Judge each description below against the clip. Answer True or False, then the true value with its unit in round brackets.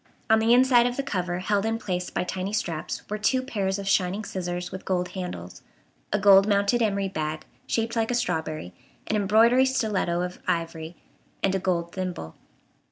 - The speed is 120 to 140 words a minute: False (180 wpm)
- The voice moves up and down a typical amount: True (3.7 semitones)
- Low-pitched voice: False (195 Hz)